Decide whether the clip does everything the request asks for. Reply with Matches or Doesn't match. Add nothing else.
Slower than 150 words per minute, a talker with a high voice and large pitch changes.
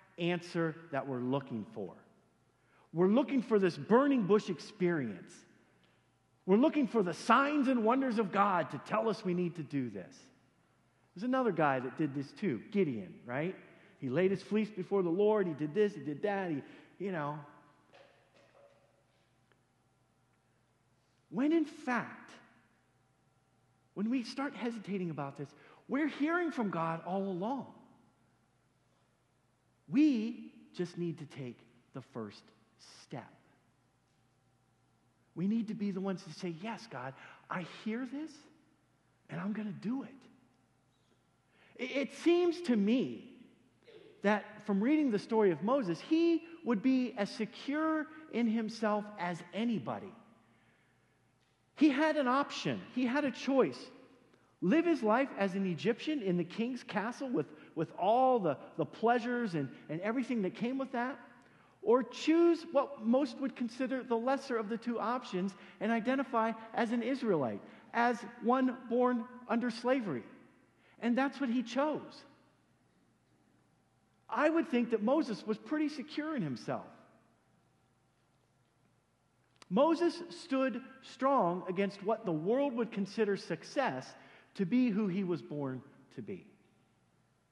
Matches